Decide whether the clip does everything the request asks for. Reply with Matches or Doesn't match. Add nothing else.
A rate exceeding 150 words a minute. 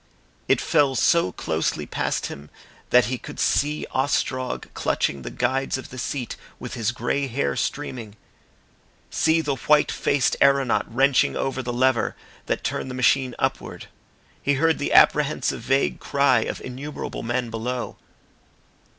Doesn't match